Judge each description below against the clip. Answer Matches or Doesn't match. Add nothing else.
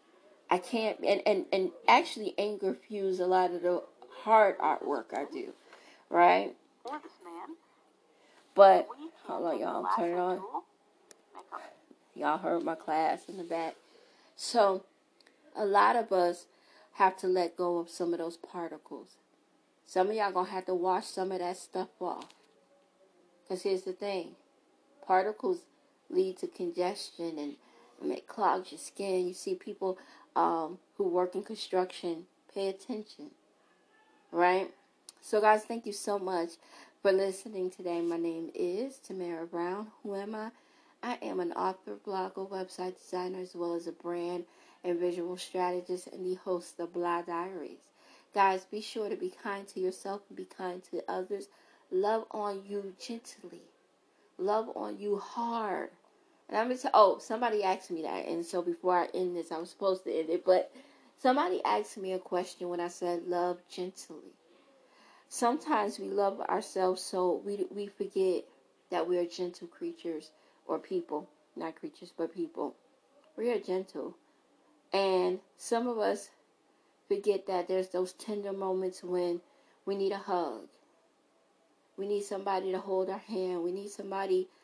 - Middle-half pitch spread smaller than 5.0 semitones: Matches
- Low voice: Doesn't match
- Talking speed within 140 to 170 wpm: Matches